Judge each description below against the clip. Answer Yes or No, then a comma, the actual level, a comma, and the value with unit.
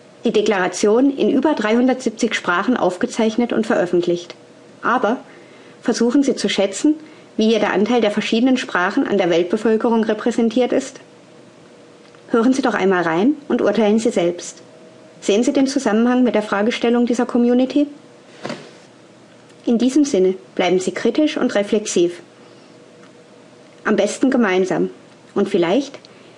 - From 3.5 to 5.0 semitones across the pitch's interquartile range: Yes, average, 3.8 semitones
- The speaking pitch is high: Yes, high, 230 Hz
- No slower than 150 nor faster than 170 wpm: No, average, 130 wpm